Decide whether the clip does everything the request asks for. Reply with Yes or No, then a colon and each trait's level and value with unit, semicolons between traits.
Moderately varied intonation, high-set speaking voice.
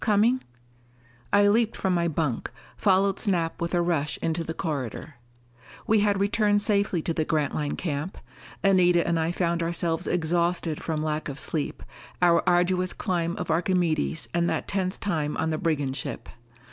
No: average, 3.2 semitones; medium, 170 Hz